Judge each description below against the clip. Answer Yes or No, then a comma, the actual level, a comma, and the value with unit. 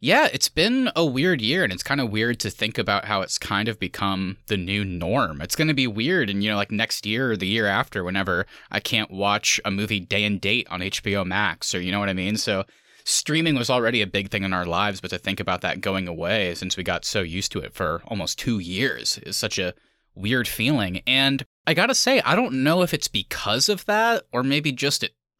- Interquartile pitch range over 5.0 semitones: Yes, wide, 5.4 semitones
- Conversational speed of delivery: No, fast, 250 wpm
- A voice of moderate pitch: No, low, 105 Hz